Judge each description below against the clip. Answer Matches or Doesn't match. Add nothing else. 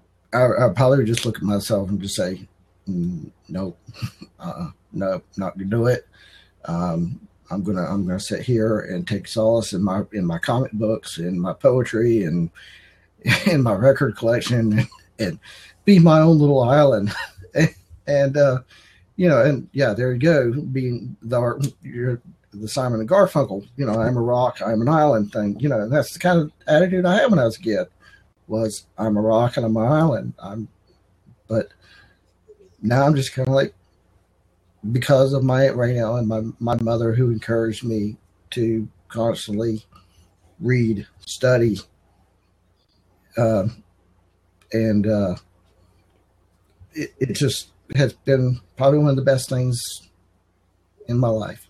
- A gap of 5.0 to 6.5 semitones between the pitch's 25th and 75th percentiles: Matches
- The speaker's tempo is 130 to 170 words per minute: Matches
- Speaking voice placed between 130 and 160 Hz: Doesn't match